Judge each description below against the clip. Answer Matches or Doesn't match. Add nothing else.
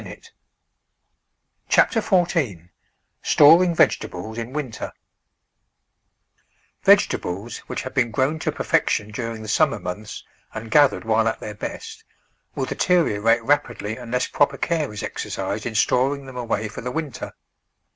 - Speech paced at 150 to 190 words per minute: Doesn't match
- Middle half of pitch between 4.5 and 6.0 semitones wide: Matches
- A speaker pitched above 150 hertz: Doesn't match